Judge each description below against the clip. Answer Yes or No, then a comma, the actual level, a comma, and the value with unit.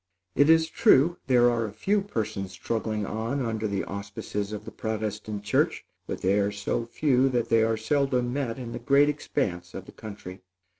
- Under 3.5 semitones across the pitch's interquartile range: No, average, 4.6 semitones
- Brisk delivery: No, average, 190 wpm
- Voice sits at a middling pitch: No, low, 115 Hz